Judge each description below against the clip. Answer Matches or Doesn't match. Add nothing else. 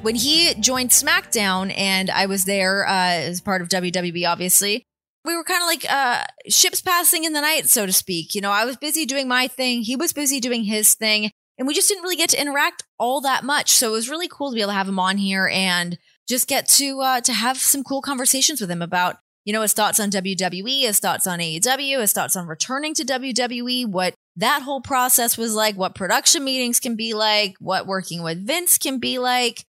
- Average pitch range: Doesn't match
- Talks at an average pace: Doesn't match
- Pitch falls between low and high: Doesn't match